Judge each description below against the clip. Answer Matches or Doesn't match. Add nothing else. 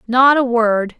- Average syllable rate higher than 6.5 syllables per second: Doesn't match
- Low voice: Doesn't match